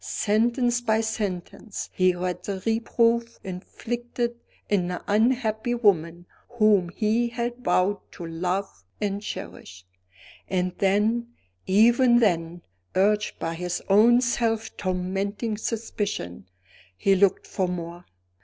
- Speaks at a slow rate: Yes, slow, 115 wpm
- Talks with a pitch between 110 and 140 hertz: No, high, 205 Hz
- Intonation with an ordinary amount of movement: Yes, average, 4.3 semitones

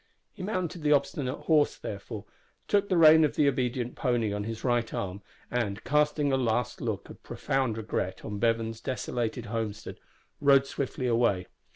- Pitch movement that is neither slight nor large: Yes, average, 4.5 semitones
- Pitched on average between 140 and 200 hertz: No, low, 125 Hz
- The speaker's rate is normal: Yes, average, 165 wpm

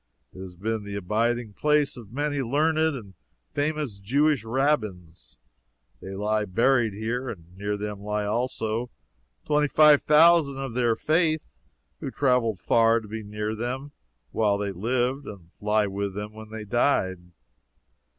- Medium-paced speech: Yes, average, 150 wpm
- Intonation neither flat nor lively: Yes, average, 4.9 semitones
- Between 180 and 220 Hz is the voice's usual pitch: No, low, 115 Hz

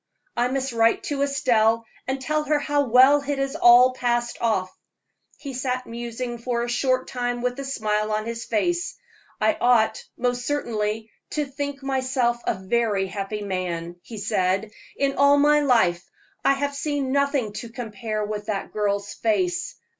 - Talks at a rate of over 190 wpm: No, average, 165 wpm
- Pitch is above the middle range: Yes, high, 240 Hz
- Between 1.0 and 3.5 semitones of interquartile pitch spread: No, average, 4.2 semitones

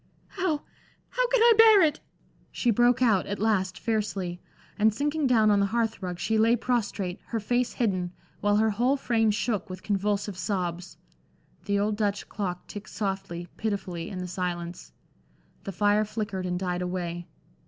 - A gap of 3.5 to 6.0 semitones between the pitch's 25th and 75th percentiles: Yes, average, 3.8 semitones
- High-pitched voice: Yes, high, 205 Hz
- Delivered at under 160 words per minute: No, average, 165 wpm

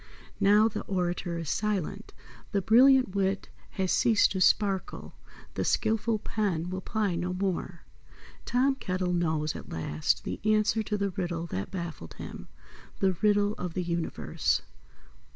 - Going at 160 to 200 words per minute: No, average, 145 wpm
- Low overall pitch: No, high, 190 Hz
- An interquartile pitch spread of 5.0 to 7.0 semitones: No, average, 3.4 semitones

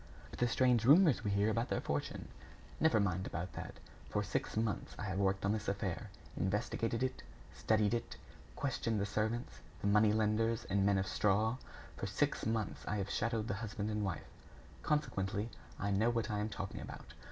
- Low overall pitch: Yes, low, 105 Hz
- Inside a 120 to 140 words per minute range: No, average, 185 wpm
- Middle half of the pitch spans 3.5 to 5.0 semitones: No, narrow, 2.4 semitones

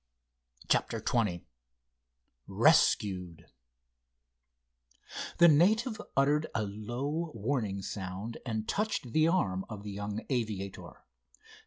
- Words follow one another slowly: Yes, slow, 95 wpm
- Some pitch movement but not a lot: No, wide, 7.0 semitones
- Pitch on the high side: No, low, 110 Hz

